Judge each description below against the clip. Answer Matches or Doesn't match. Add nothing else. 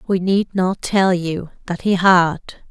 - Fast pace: Doesn't match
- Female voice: Matches